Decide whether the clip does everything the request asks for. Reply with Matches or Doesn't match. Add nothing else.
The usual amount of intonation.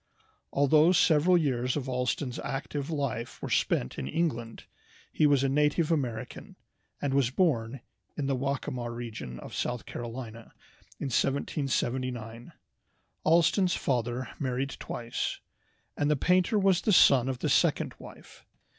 Matches